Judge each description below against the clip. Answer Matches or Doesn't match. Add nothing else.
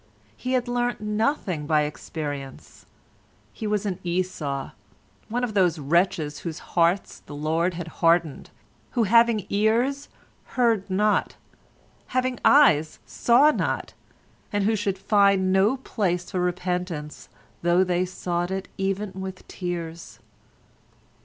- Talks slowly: Matches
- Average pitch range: Matches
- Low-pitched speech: Doesn't match